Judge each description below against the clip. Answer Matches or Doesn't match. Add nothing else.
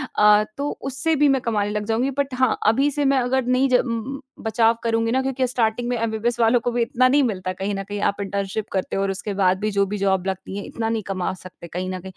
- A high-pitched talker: Matches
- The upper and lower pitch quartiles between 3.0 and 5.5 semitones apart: Matches